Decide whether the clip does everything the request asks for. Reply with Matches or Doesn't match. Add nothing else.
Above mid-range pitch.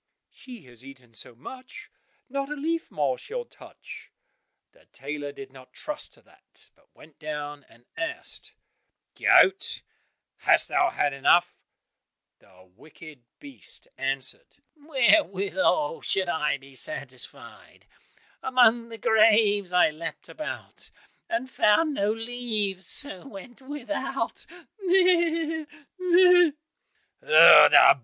Matches